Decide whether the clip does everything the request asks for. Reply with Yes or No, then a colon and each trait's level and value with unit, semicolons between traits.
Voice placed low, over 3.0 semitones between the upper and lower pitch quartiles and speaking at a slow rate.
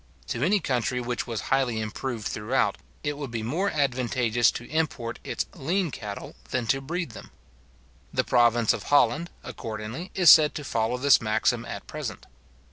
No: low, 125 Hz; average, 4.3 semitones; average, 165 wpm